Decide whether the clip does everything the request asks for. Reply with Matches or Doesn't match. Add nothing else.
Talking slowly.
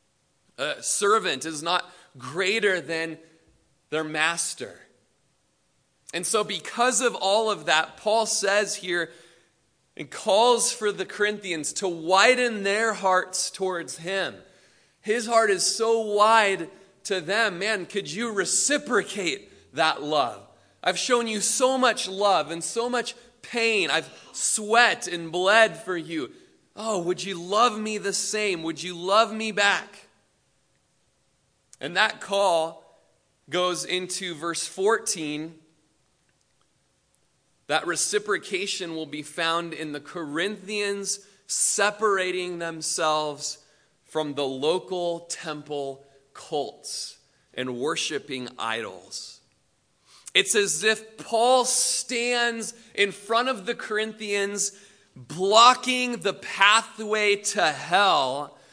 Matches